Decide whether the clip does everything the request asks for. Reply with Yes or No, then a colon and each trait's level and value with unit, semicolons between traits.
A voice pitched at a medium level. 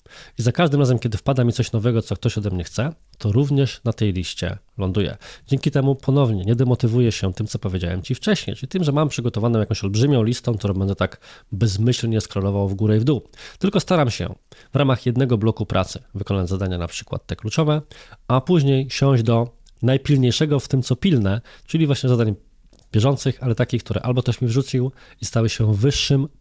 No: low, 120 Hz